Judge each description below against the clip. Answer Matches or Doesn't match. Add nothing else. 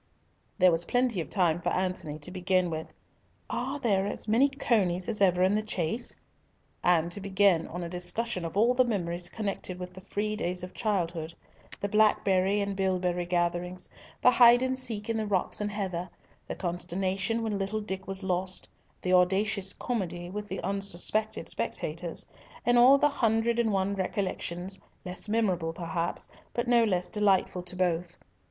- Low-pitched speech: Doesn't match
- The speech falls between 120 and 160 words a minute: Doesn't match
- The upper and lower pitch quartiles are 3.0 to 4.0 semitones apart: Matches